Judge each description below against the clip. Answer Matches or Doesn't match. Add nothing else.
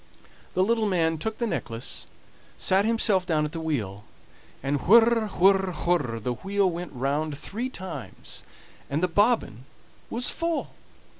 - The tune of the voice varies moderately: Doesn't match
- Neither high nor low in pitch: Matches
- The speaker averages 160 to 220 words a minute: Doesn't match